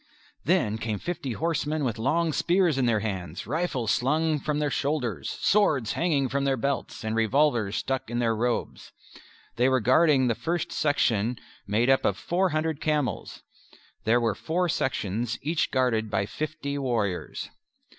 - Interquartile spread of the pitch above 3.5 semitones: Yes, wide, 5.4 semitones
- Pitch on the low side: Yes, low, 130 Hz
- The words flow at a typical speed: Yes, average, 155 wpm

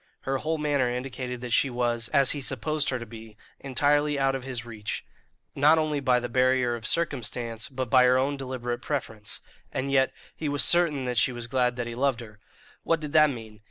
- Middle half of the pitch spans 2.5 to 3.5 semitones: Yes, average, 2.9 semitones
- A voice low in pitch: Yes, low, 130 Hz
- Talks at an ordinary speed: No, fast, 210 wpm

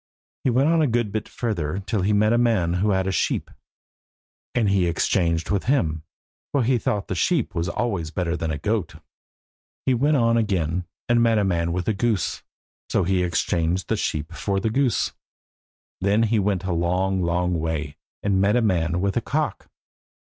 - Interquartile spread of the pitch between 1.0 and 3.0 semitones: No, average, 4.8 semitones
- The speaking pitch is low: Yes, very low, 95 Hz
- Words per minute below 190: No, average, 195 wpm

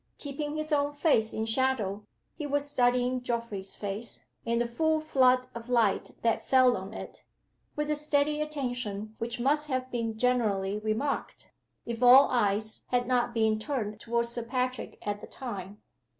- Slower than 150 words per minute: No, average, 165 wpm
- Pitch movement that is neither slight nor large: Yes, average, 3.8 semitones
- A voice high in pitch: Yes, high, 245 Hz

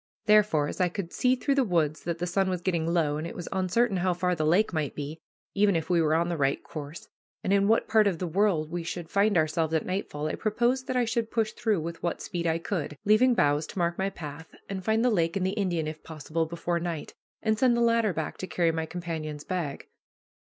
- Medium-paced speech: No, fast, 245 wpm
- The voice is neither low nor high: Yes, medium, 175 Hz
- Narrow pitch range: No, average, 4.3 semitones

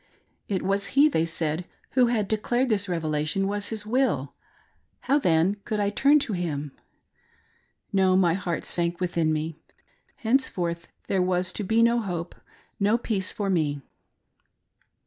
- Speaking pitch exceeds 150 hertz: Yes, high, 190 Hz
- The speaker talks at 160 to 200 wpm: No, average, 150 wpm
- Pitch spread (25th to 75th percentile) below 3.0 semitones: No, average, 4.5 semitones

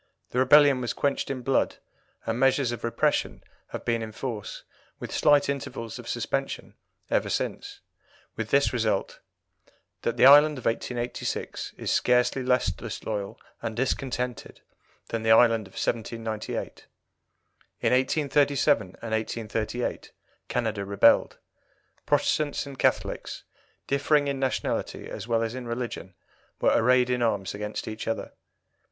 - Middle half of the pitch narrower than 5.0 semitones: Yes, average, 3.2 semitones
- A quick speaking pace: No, slow, 135 wpm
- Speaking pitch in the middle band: No, low, 120 Hz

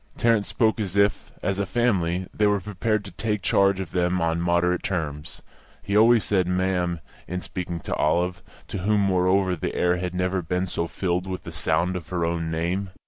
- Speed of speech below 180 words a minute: No, average, 195 wpm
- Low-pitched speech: Yes, very low, 90 Hz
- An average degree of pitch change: No, narrow, 2.3 semitones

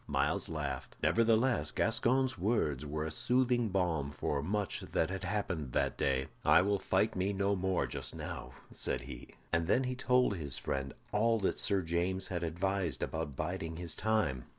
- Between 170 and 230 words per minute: Yes, average, 175 wpm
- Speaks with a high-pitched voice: No, very low, 95 Hz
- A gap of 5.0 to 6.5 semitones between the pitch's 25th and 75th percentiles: Yes, wide, 5.5 semitones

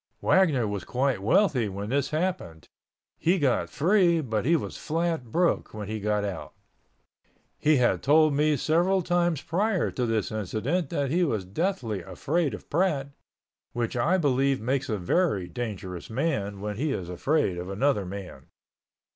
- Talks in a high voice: No, low, 135 Hz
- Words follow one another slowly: No, average, 160 wpm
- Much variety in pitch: Yes, wide, 7.7 semitones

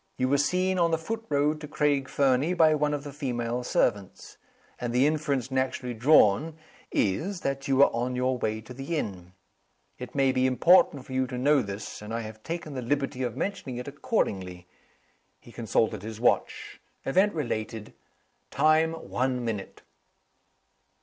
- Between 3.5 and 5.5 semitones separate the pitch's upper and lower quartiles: Yes, average, 4.1 semitones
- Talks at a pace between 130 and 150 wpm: No, average, 170 wpm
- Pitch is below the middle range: Yes, low, 130 Hz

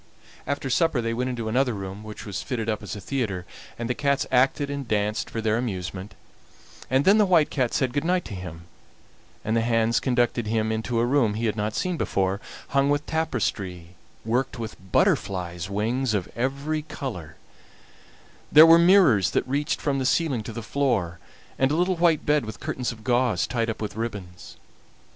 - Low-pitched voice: Yes, low, 120 Hz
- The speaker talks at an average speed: Yes, average, 190 wpm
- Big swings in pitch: No, average, 4.8 semitones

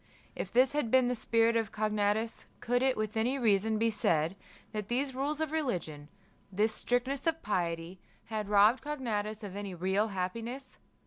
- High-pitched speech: Yes, high, 220 Hz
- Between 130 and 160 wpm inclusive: No, average, 170 wpm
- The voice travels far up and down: No, average, 3.8 semitones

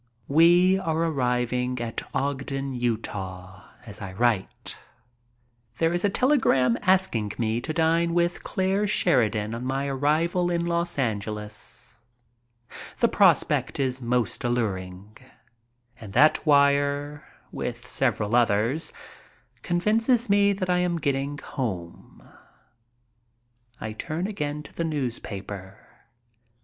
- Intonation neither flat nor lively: No, wide, 7.1 semitones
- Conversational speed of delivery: No, slow, 115 wpm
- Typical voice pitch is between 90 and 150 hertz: Yes, low, 135 Hz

